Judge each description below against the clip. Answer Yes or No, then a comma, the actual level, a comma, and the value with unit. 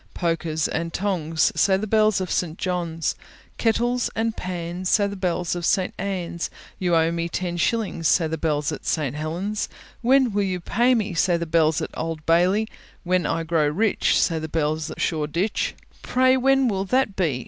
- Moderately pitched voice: Yes, medium, 175 Hz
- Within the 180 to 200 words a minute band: Yes, average, 185 wpm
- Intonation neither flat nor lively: Yes, average, 3.9 semitones